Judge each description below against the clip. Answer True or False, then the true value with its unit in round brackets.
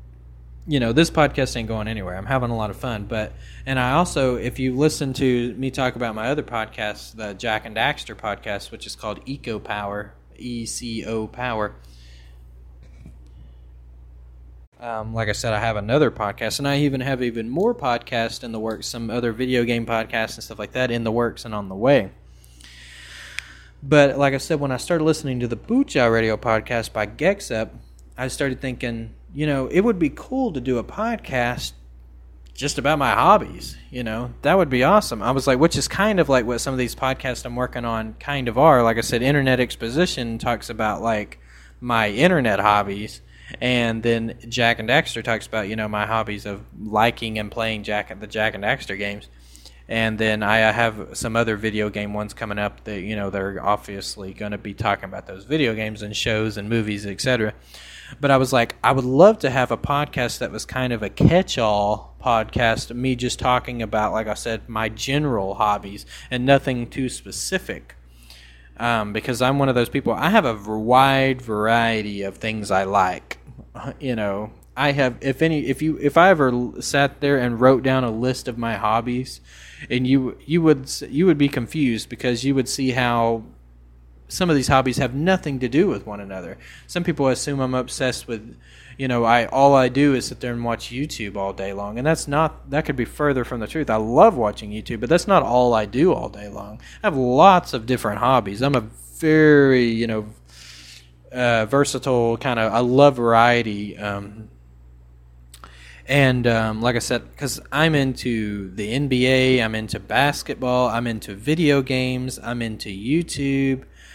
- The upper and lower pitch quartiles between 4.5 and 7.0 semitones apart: False (4.0 semitones)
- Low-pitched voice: True (115 Hz)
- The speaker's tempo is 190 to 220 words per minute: True (195 wpm)